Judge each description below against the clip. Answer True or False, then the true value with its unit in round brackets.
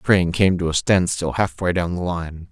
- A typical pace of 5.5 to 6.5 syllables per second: False (5.3 syllables/s)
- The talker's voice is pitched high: False (90 Hz)